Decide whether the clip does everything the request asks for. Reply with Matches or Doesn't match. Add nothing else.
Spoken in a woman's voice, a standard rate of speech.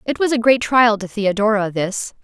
Doesn't match